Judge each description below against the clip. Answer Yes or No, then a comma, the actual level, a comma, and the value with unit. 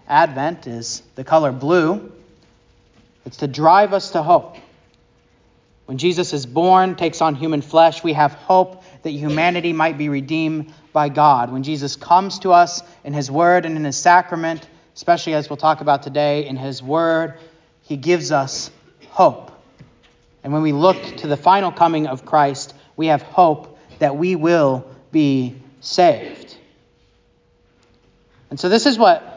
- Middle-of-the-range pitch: Yes, medium, 155 Hz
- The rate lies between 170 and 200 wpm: No, average, 155 wpm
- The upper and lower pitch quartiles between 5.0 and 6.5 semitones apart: No, average, 3.4 semitones